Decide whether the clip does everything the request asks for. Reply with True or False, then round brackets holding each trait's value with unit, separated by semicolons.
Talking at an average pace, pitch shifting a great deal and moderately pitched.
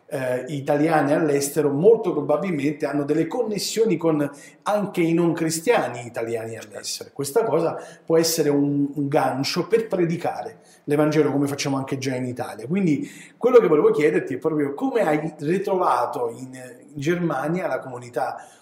False (150 wpm; 2.8 semitones; 155 Hz)